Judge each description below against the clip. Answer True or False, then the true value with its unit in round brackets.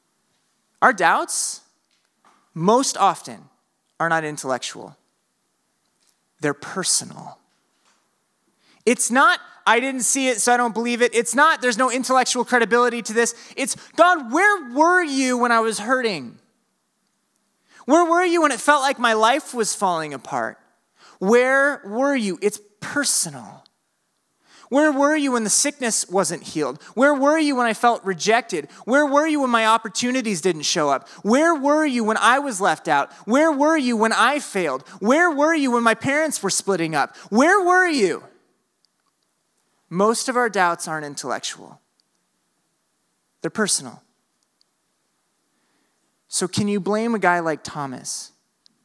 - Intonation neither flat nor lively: False (5.9 semitones)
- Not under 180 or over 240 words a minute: False (145 wpm)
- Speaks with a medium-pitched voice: False (240 Hz)